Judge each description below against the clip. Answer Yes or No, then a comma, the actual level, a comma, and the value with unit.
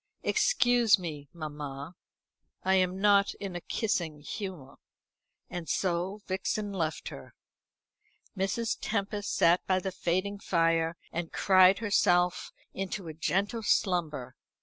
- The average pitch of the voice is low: No, medium, 185 Hz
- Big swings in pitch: No, average, 3.3 semitones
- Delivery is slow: Yes, slow, 120 wpm